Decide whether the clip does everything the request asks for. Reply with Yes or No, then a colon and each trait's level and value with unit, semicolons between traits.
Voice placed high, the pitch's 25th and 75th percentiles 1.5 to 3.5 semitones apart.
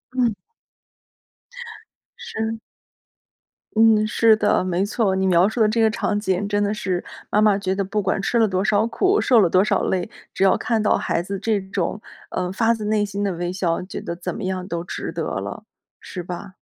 Yes: high, 200 Hz; average, 2.7 semitones